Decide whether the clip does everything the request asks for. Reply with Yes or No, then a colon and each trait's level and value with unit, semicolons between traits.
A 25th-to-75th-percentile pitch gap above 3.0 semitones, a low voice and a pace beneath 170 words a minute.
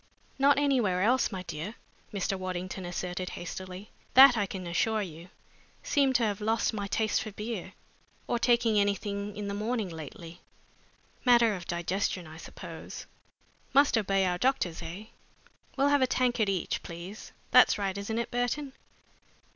No: average, 4.4 semitones; high, 205 Hz; average, 155 wpm